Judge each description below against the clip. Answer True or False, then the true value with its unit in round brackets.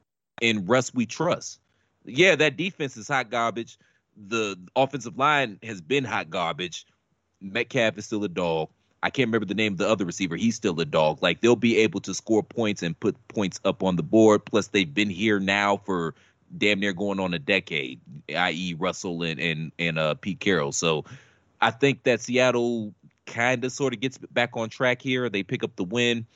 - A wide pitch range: False (4.1 semitones)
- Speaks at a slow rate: False (200 wpm)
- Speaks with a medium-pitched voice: False (110 Hz)